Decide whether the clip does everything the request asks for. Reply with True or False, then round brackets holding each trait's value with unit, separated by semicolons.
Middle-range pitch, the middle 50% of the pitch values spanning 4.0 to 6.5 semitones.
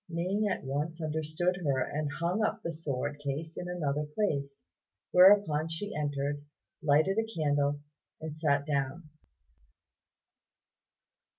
False (155 Hz; 3.3 semitones)